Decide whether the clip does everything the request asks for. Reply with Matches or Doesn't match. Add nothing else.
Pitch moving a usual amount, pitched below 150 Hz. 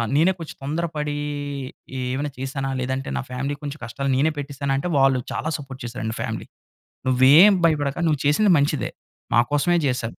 Doesn't match